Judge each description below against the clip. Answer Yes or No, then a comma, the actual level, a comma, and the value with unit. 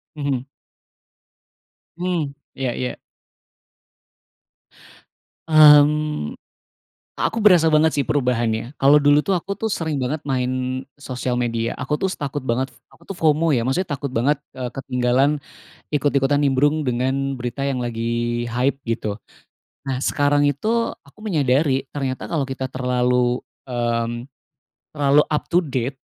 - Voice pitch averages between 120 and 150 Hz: Yes, low, 135 Hz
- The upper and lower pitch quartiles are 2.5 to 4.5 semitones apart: Yes, average, 3.0 semitones